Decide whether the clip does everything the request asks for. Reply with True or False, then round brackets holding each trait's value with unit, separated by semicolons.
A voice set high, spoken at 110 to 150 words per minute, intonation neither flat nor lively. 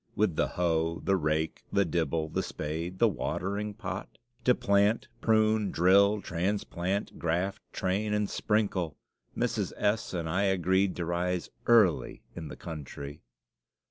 False (95 Hz; 140 wpm; 3.5 semitones)